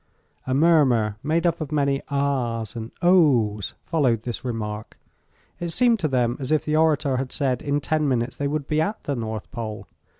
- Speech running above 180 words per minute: Yes, average, 190 wpm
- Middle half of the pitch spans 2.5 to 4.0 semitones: No, average, 4.8 semitones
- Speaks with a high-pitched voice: No, medium, 140 Hz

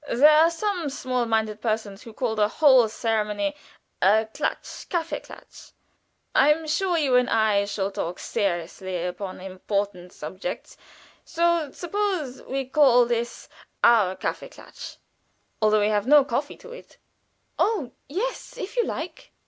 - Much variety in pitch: Yes, wide, 6.8 semitones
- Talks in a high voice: Yes, high, 240 Hz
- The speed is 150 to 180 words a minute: No, average, 140 wpm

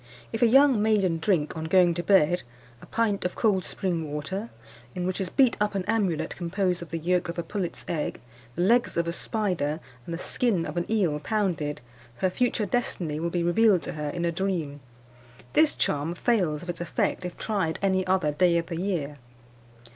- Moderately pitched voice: Yes, medium, 180 Hz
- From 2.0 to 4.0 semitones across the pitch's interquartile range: Yes, average, 3.5 semitones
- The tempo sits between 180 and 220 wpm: Yes, fast, 205 wpm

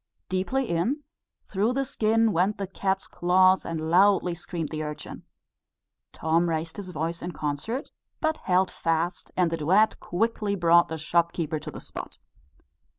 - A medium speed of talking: Yes, average, 155 wpm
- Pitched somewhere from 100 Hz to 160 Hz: No, medium, 180 Hz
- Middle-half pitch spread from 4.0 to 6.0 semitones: No, average, 3.5 semitones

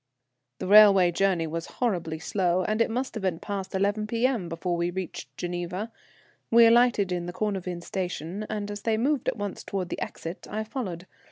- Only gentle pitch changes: No, average, 3.6 semitones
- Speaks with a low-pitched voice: No, high, 195 Hz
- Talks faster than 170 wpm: Yes, average, 185 wpm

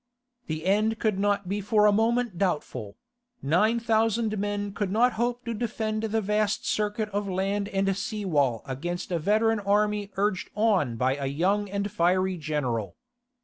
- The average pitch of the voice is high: Yes, high, 205 Hz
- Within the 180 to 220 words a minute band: No, average, 170 wpm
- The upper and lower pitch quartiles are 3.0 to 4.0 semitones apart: Yes, average, 3.3 semitones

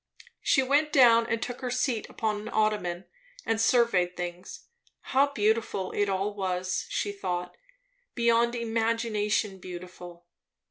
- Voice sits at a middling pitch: No, high, 215 Hz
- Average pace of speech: No, slow, 130 wpm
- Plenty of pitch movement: No, average, 4.1 semitones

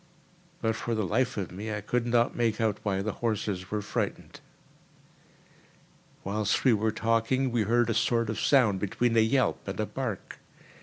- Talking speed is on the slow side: No, average, 175 wpm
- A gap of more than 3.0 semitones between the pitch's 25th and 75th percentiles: No, narrow, 2.4 semitones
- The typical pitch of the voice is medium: No, low, 110 Hz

